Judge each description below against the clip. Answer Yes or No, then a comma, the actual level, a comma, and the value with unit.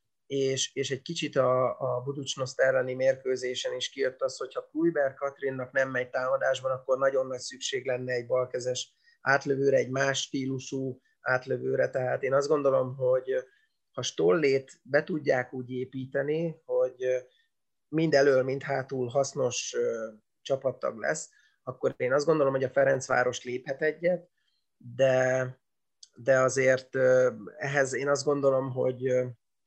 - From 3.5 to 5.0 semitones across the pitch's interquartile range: No, average, 2.8 semitones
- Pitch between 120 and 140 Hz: Yes, low, 135 Hz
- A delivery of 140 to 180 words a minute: No, average, 130 wpm